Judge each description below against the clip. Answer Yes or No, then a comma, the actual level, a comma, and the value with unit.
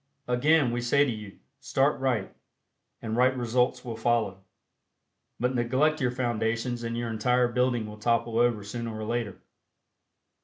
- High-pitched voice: No, low, 120 Hz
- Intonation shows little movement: Yes, narrow, 1.9 semitones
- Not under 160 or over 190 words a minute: No, average, 150 wpm